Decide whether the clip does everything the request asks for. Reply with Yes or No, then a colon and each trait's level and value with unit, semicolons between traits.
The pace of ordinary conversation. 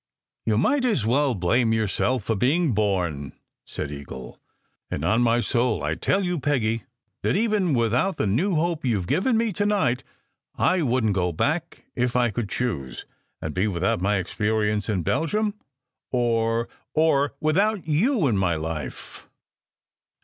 Yes: average, 170 wpm